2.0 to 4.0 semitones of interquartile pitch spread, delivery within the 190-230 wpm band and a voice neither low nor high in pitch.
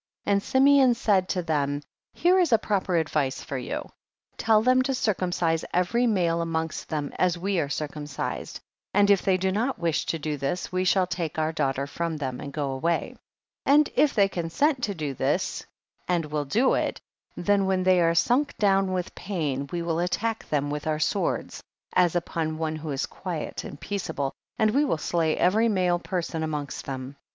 No: average, 4.6 semitones; average, 195 wpm; medium, 175 Hz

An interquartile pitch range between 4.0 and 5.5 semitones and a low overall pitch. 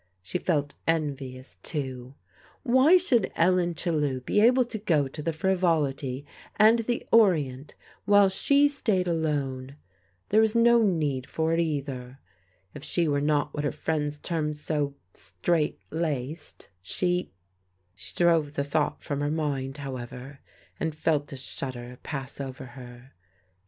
No: average, 4.6 semitones; medium, 150 Hz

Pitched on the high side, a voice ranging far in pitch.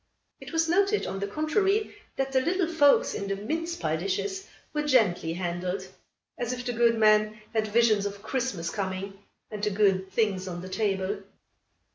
Yes: high, 215 Hz; wide, 6.6 semitones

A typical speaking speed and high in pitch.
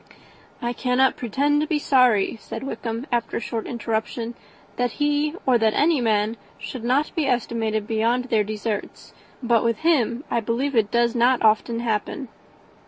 Yes: average, 165 wpm; high, 235 Hz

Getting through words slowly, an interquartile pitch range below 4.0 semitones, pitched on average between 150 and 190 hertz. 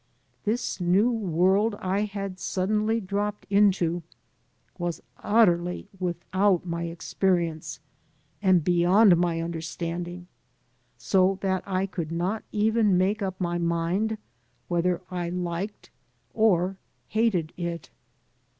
Yes: slow, 105 wpm; average, 2.8 semitones; medium, 185 Hz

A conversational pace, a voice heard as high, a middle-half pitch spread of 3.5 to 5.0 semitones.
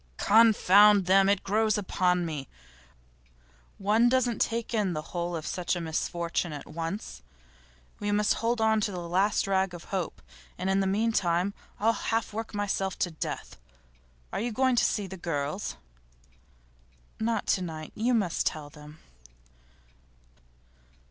Yes: average, 150 wpm; high, 195 Hz; average, 3.9 semitones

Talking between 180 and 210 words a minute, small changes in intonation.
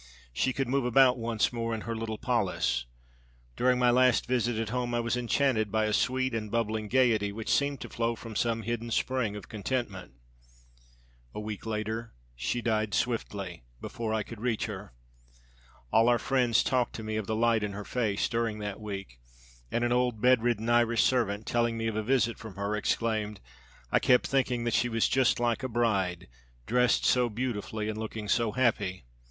Yes: average, 190 wpm; narrow, 2.3 semitones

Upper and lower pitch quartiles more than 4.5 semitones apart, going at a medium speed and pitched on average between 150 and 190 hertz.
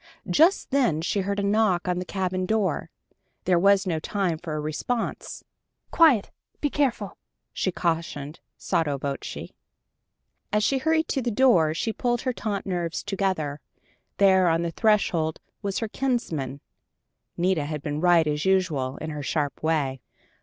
Yes: average, 5.1 semitones; average, 155 wpm; medium, 185 Hz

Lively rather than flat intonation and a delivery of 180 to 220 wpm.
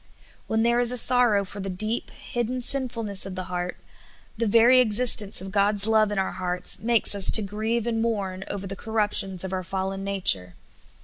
No: average, 3.2 semitones; average, 200 wpm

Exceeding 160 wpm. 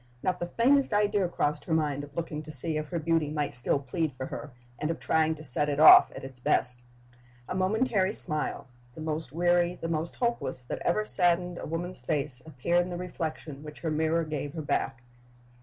Yes: fast, 205 wpm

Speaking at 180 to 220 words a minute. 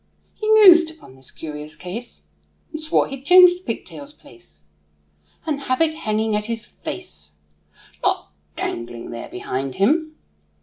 No: average, 140 wpm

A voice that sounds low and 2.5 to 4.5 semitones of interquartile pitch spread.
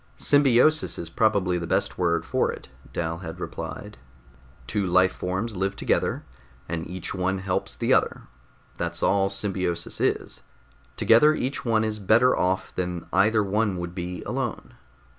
Yes: very low, 95 Hz; average, 3.6 semitones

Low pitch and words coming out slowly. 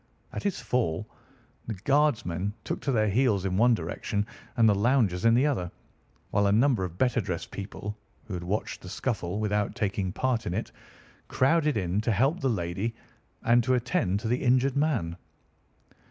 No: low, 110 Hz; average, 180 wpm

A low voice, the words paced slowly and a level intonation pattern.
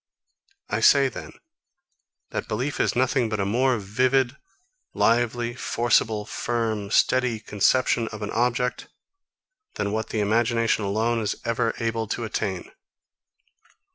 Yes: low, 115 Hz; slow, 125 wpm; narrow, 2.1 semitones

